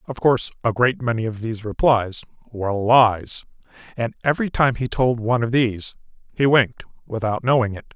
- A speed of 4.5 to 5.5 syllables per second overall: No, 5.8 syllables/s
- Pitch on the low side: Yes, low, 120 Hz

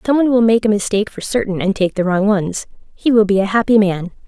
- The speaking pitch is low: No, high, 205 Hz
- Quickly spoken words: Yes, fast, 255 wpm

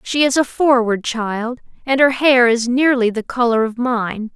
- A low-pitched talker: No, high, 245 Hz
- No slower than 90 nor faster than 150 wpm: No, average, 195 wpm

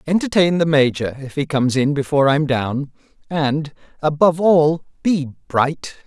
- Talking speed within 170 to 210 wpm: No, average, 150 wpm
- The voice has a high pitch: No, medium, 150 Hz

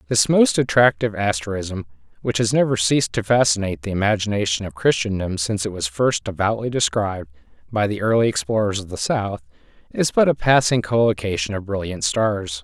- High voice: No, low, 105 Hz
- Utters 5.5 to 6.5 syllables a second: Yes, 5.7 syllables/s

